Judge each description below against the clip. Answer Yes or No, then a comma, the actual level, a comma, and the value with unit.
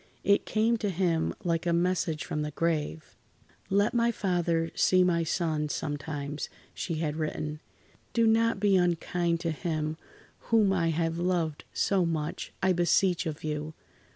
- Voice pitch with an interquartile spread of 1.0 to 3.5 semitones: Yes, average, 3.0 semitones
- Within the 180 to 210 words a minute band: No, average, 155 wpm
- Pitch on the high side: No, medium, 170 Hz